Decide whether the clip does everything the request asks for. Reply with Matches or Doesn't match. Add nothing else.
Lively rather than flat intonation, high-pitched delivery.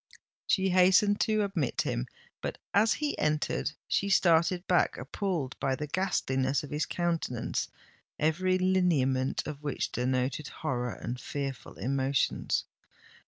Doesn't match